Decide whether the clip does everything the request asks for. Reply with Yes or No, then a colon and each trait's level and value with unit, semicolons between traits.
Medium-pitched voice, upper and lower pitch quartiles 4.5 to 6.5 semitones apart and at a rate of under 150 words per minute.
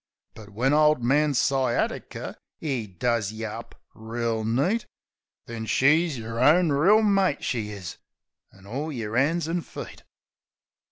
No: low, 125 Hz; wide, 5.4 semitones; slow, 135 wpm